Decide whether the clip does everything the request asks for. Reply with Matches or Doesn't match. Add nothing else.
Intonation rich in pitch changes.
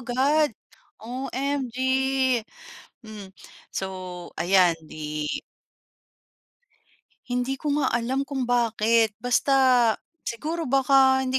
Doesn't match